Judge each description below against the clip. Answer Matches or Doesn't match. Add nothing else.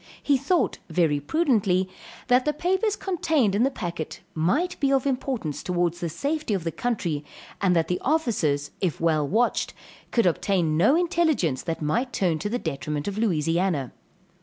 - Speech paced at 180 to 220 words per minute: Doesn't match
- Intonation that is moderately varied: Doesn't match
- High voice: Matches